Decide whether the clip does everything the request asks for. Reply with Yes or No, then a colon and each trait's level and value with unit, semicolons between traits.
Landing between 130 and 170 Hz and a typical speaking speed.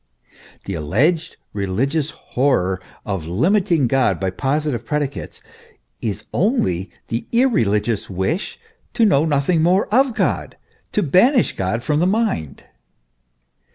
No: medium, 140 Hz; slow, 120 wpm